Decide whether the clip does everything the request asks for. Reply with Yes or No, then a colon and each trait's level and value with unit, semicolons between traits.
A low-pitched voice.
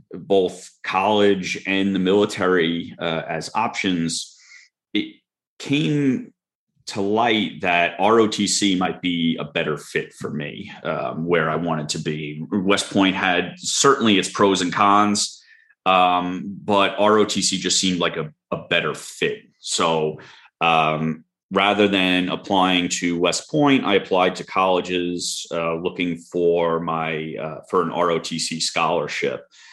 Yes: very low, 90 Hz